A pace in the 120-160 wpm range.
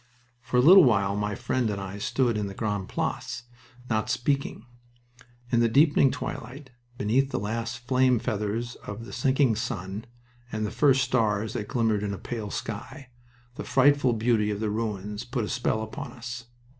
No: average, 175 wpm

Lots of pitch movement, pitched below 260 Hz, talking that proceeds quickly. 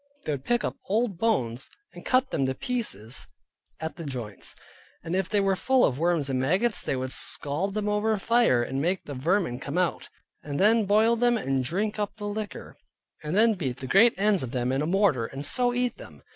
Yes: wide, 8.0 semitones; medium, 185 Hz; fast, 220 wpm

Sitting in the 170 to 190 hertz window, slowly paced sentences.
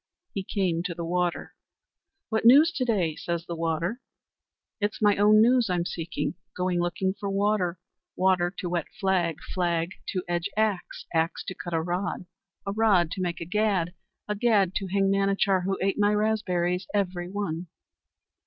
No: medium, 185 Hz; average, 170 wpm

